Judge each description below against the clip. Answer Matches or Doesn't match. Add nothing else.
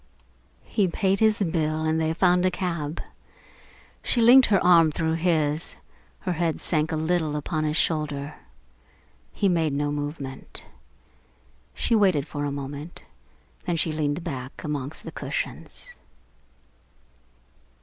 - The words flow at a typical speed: Doesn't match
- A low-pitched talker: Doesn't match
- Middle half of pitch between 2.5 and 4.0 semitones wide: Matches